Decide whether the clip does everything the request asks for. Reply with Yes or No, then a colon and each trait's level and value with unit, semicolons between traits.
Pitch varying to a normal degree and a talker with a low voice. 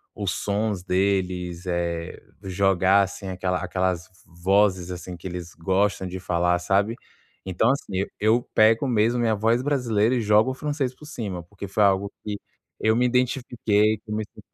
Yes: average, 3.4 semitones; low, 100 Hz